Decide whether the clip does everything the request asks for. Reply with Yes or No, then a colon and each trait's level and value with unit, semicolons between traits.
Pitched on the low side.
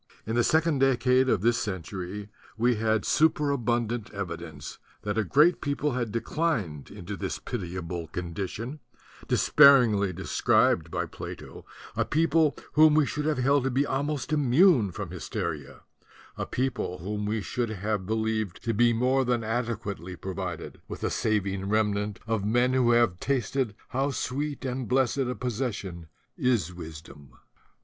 Yes: low, 115 Hz